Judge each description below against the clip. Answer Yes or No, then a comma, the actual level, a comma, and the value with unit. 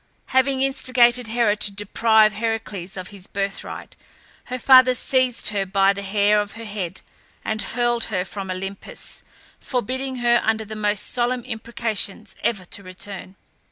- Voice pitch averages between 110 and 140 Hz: No, high, 215 Hz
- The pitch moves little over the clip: No, average, 3.3 semitones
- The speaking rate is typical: Yes, average, 150 wpm